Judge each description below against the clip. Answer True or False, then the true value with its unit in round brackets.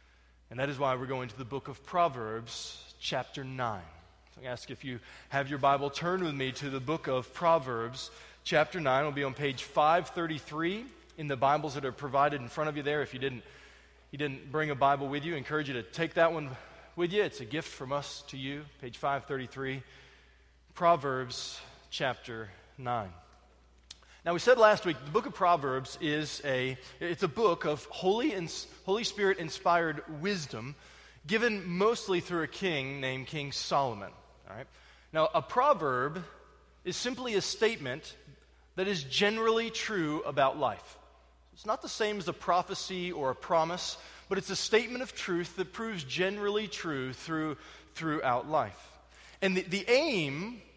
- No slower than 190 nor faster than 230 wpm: False (180 wpm)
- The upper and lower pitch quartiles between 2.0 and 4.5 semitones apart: False (5.5 semitones)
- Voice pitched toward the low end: False (150 Hz)